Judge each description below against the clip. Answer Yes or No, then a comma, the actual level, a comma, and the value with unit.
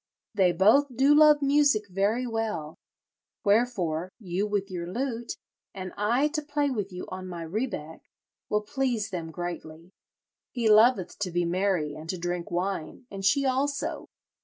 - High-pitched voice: Yes, high, 200 Hz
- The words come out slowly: No, average, 155 wpm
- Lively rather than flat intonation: Yes, wide, 5.9 semitones